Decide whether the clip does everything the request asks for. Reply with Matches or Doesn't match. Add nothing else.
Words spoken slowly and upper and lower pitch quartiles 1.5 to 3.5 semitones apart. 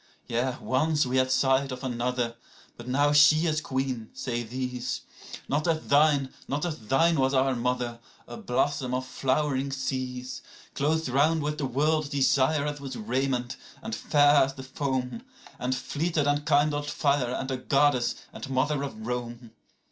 Doesn't match